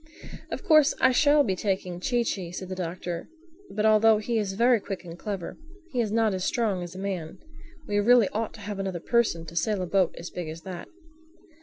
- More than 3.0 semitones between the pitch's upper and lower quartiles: Yes, average, 4.0 semitones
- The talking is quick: Yes, fast, 215 wpm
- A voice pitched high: Yes, high, 195 Hz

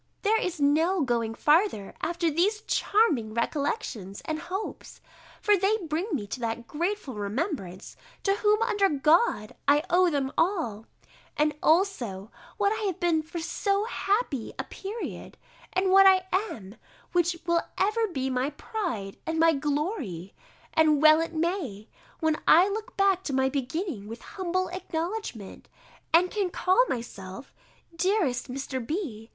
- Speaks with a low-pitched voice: No, very high, 325 Hz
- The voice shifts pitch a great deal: Yes, wide, 7.0 semitones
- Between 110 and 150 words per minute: Yes, average, 145 wpm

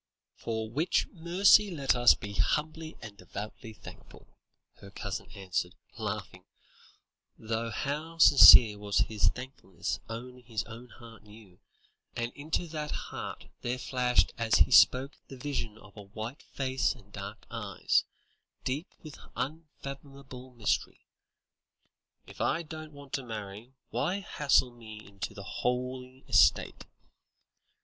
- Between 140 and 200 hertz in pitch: No, low, 125 Hz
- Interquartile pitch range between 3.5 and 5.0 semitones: Yes, average, 4.6 semitones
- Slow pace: Yes, slow, 130 wpm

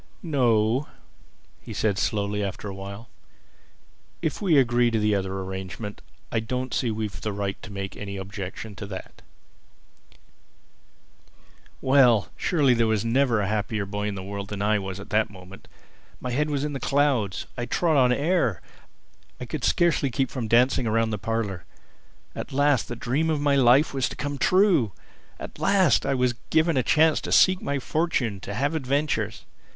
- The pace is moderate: Yes, average, 180 wpm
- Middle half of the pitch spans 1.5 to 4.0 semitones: No, wide, 5.4 semitones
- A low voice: Yes, low, 115 Hz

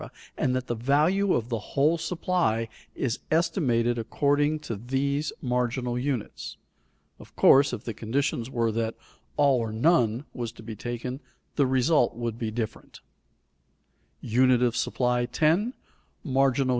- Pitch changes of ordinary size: Yes, average, 3.7 semitones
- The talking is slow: Yes, slow, 120 wpm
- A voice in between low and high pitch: No, low, 125 Hz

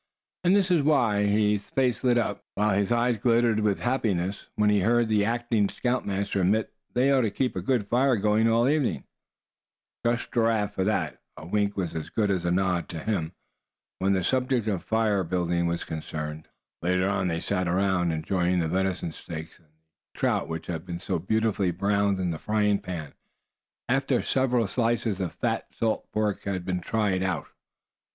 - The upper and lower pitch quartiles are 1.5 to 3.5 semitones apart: No, average, 4.2 semitones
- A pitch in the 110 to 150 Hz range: No, low, 100 Hz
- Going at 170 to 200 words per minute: Yes, average, 185 wpm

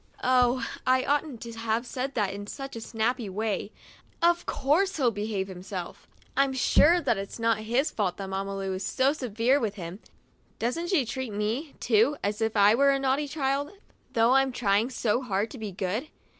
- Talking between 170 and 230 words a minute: Yes, average, 190 wpm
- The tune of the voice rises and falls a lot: No, average, 4.7 semitones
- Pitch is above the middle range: Yes, high, 235 Hz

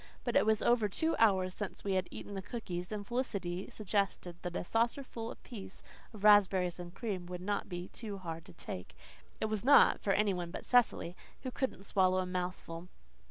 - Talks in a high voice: Yes, high, 195 Hz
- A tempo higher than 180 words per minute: Yes, average, 190 wpm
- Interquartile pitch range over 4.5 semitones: No, average, 3.3 semitones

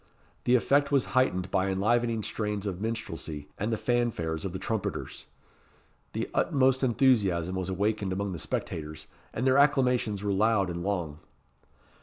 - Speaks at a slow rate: No, average, 150 wpm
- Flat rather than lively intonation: No, average, 4.5 semitones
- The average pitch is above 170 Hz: No, low, 105 Hz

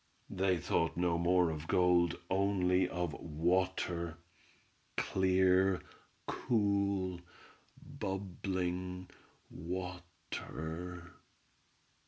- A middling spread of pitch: No, narrow, 1.4 semitones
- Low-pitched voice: Yes, very low, 90 Hz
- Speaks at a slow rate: Yes, slow, 60 wpm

